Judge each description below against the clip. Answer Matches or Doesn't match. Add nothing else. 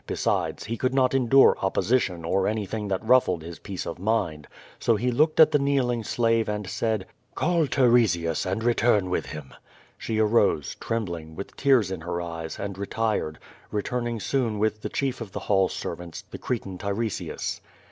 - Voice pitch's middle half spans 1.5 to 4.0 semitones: Doesn't match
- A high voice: Doesn't match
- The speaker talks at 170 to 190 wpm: Matches